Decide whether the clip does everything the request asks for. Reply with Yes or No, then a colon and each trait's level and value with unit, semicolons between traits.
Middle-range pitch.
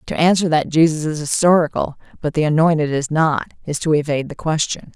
Yes: medium, 155 Hz